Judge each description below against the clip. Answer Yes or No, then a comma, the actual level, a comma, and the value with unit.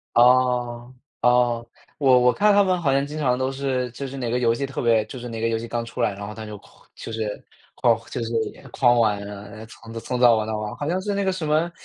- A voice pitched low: Yes, low, 125 Hz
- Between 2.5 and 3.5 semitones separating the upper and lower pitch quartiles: Yes, average, 3.2 semitones